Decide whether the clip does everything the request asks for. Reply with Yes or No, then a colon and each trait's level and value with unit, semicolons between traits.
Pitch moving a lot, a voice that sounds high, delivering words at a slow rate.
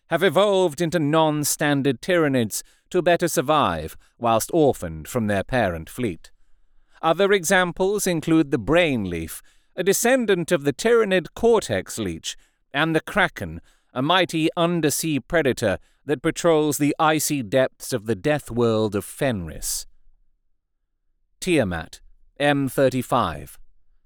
No: wide, 7.7 semitones; medium, 150 Hz; slow, 120 wpm